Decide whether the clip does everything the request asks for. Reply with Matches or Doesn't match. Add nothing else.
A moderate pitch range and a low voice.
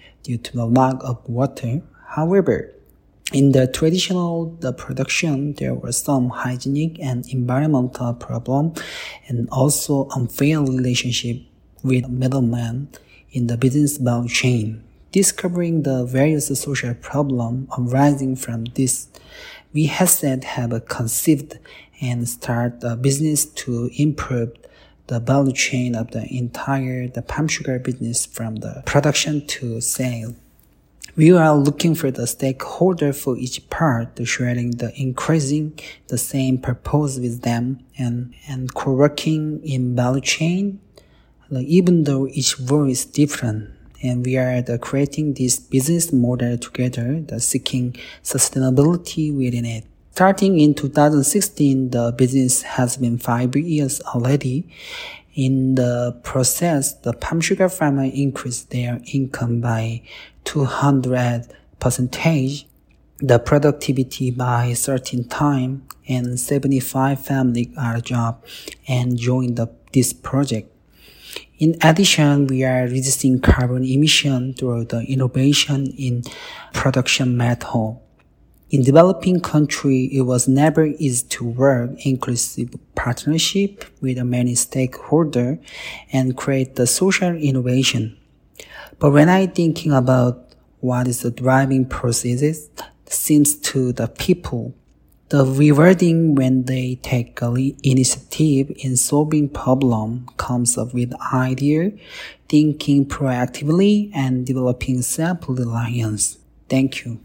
Matches